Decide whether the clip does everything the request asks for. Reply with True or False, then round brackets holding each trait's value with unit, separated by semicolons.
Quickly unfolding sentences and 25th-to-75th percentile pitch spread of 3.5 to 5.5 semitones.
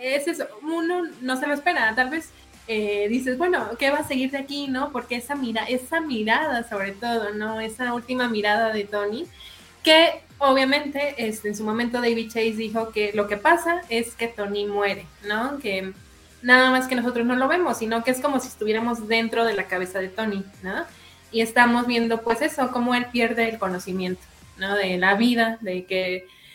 True (195 wpm; 3.8 semitones)